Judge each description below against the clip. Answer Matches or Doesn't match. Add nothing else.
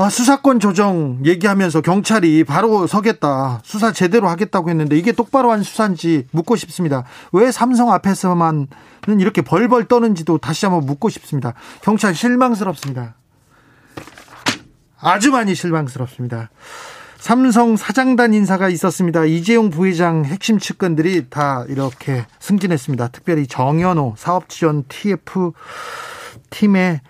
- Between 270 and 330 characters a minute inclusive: Matches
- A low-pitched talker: Doesn't match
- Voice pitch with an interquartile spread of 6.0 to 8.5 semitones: Matches